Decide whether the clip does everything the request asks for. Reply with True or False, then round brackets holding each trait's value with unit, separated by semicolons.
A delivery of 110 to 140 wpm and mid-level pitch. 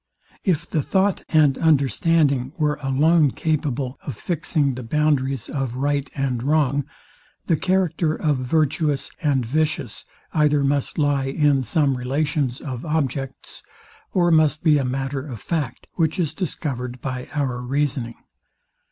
True (135 wpm; 145 Hz)